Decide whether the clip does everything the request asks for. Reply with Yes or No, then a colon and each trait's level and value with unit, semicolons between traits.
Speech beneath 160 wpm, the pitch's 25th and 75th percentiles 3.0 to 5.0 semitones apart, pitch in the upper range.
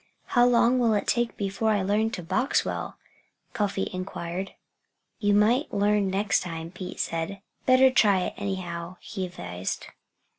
Yes: average, 150 wpm; average, 3.3 semitones; high, 200 Hz